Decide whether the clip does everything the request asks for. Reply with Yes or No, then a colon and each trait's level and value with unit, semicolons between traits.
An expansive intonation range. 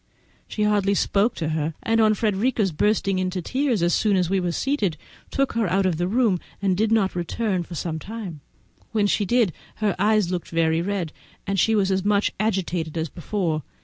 No: average, 3.6 semitones